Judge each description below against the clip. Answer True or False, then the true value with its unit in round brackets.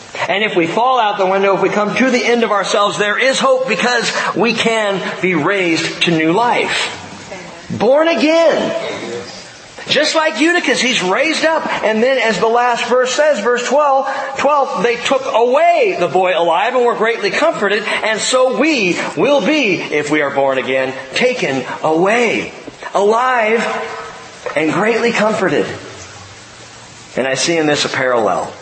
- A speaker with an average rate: True (160 wpm)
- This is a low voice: False (225 Hz)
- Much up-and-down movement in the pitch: True (6.5 semitones)